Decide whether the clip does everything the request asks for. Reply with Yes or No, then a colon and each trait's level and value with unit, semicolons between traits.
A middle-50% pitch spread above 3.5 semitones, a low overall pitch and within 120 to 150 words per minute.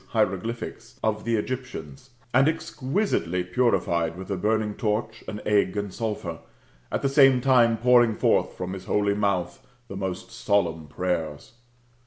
Yes: average, 4.7 semitones; low, 105 Hz; average, 145 wpm